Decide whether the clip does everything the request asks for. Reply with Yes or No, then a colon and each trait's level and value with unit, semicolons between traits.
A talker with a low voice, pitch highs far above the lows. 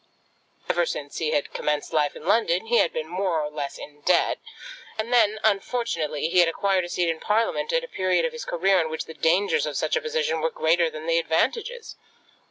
No: medium, 180 Hz; wide, 6.2 semitones